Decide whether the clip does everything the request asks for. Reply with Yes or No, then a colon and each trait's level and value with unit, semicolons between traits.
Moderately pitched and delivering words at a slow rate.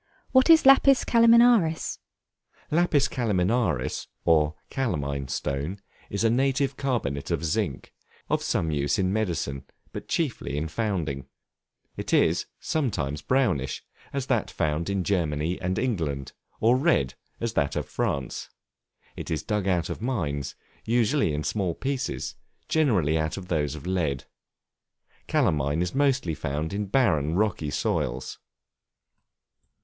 No: very low, 90 Hz; slow, 130 wpm